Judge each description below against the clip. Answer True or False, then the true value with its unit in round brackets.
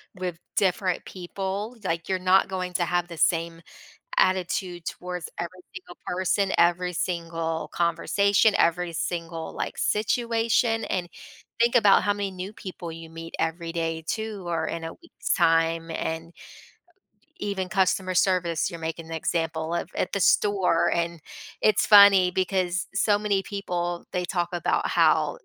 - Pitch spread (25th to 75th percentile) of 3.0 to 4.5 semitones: False (2.5 semitones)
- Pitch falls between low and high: True (180 Hz)